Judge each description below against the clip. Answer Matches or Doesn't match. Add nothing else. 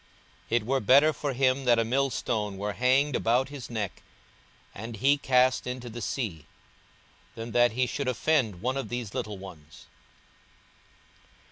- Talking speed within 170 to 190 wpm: Doesn't match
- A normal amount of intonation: Matches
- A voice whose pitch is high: Doesn't match